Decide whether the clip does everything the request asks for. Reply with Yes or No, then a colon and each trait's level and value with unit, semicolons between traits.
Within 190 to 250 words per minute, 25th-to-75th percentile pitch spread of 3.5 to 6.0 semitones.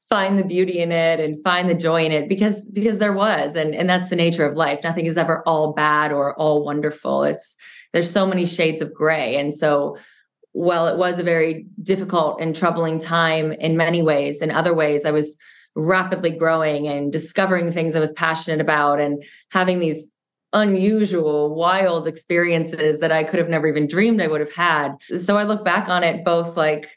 No: average, 200 wpm; average, 2.7 semitones